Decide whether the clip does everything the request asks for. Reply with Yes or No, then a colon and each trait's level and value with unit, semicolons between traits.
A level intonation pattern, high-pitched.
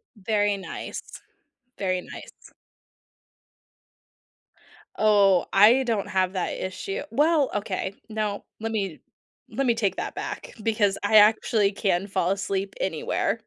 Yes: narrow, 2.1 semitones; high, 205 Hz